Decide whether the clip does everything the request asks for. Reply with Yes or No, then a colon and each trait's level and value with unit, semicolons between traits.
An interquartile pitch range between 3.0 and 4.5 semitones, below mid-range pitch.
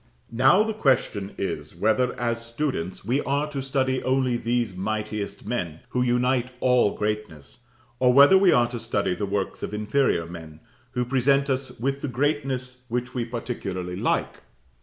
Yes: average, 3.9 semitones; low, 120 Hz